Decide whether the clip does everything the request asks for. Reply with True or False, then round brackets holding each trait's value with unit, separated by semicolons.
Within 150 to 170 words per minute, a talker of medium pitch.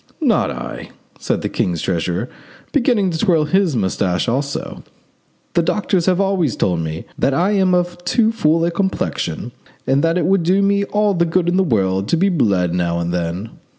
False (190 wpm; 165 Hz)